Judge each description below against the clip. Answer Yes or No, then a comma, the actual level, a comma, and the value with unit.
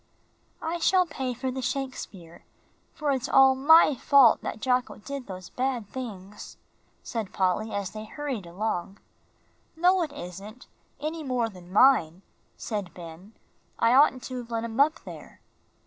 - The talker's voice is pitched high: Yes, high, 245 Hz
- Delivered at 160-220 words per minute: No, average, 150 wpm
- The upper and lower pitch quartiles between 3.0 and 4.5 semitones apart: No, wide, 5.4 semitones